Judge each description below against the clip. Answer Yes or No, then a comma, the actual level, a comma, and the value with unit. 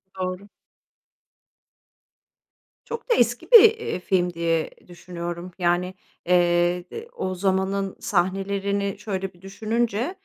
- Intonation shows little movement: Yes, narrow, 2.2 semitones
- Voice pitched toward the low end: No, high, 190 Hz